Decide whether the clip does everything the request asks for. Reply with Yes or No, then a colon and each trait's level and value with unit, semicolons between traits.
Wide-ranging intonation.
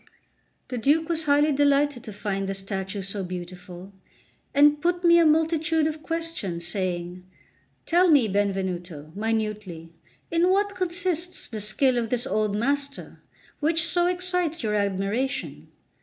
Yes: wide, 8.8 semitones